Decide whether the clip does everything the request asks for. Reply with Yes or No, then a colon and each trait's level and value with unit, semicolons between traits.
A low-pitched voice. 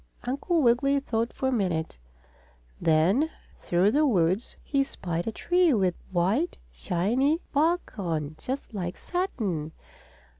No: high, 225 Hz